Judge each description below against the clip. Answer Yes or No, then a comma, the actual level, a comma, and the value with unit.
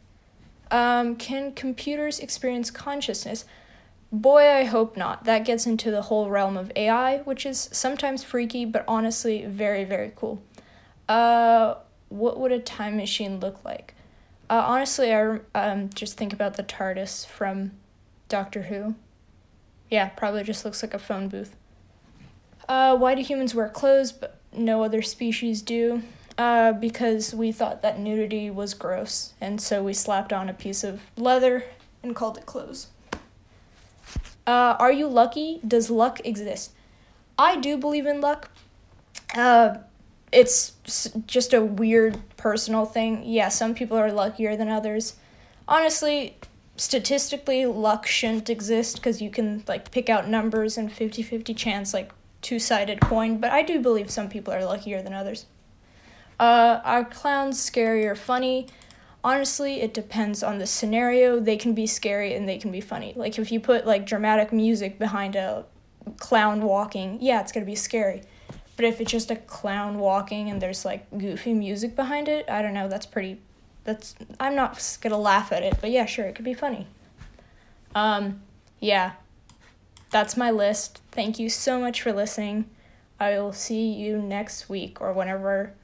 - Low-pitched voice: No, high, 225 Hz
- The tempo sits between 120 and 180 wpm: Yes, average, 160 wpm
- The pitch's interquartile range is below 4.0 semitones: Yes, average, 2.8 semitones